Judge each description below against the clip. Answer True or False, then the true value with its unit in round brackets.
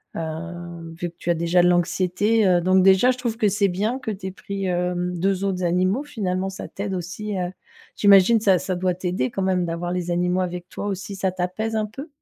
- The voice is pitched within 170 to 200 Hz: True (185 Hz)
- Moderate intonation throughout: False (2.1 semitones)